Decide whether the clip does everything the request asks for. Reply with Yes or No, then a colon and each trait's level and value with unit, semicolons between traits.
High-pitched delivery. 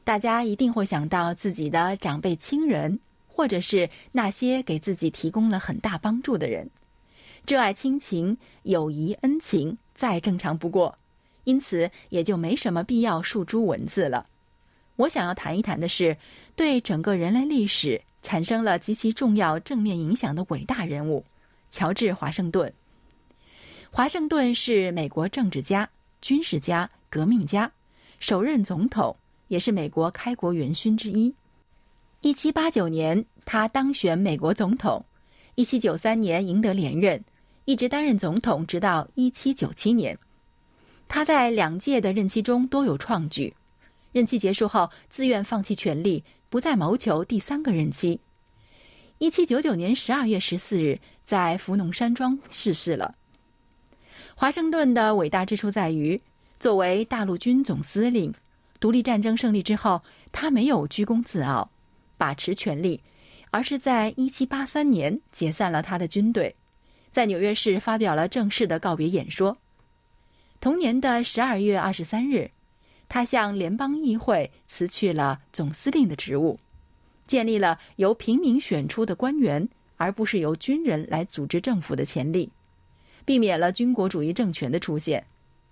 Yes: high, 210 Hz